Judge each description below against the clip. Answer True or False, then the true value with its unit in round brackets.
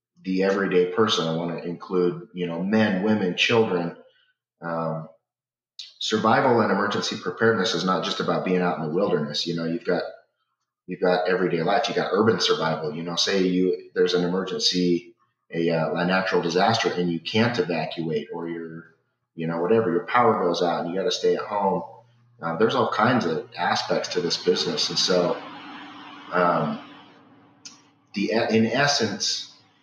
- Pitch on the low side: True (90 Hz)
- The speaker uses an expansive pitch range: False (2.8 semitones)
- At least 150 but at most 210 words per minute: True (170 wpm)